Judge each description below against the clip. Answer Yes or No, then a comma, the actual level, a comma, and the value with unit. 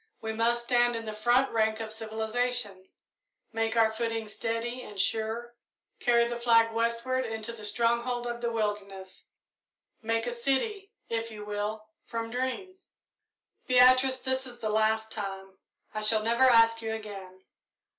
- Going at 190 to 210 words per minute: No, average, 150 wpm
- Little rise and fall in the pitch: Yes, narrow, 1.8 semitones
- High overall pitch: Yes, high, 230 Hz